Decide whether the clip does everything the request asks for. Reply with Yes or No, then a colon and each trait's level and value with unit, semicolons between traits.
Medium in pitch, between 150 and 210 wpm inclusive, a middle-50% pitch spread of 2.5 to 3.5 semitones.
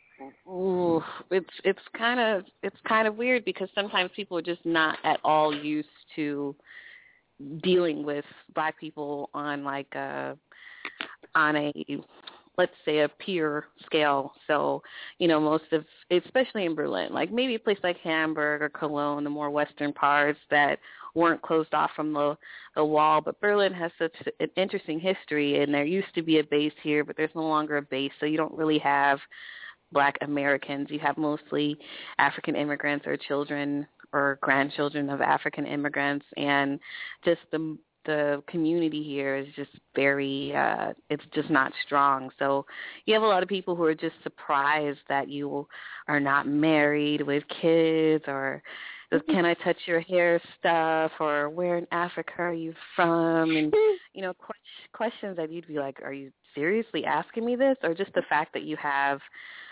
Yes: medium, 155 Hz; average, 170 wpm; average, 3.0 semitones